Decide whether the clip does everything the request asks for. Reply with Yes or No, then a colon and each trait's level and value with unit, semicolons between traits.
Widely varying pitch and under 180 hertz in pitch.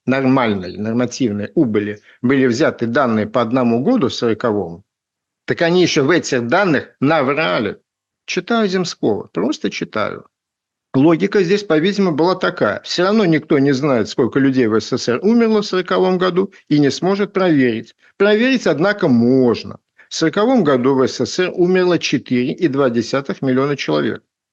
Yes: wide, 7.1 semitones; medium, 140 Hz